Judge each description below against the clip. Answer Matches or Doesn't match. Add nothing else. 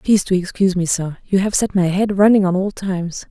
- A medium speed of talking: Doesn't match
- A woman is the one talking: Matches